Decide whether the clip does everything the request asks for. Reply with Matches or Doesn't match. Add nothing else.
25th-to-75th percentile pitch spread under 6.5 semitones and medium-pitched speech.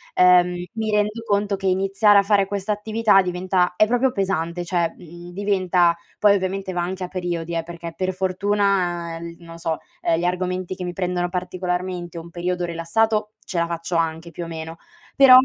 Matches